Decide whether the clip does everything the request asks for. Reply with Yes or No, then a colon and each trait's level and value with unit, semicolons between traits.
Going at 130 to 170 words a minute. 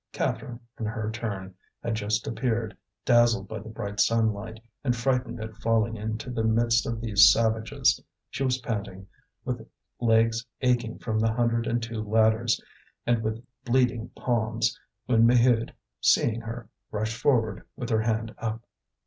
Yes: average, 150 wpm